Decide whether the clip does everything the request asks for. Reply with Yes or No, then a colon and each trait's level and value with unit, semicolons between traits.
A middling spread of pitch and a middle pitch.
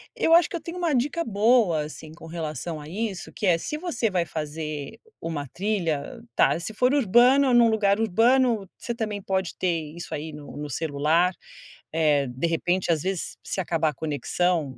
No: wide, 6.5 semitones; medium, 180 Hz